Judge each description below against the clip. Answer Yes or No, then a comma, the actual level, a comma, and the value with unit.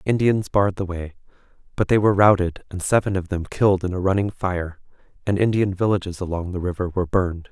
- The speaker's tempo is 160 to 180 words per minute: No, average, 200 wpm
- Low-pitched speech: Yes, very low, 95 Hz